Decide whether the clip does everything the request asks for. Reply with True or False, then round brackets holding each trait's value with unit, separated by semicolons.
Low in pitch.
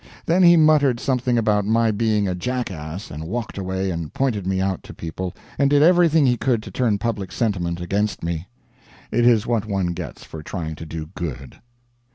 True (105 Hz)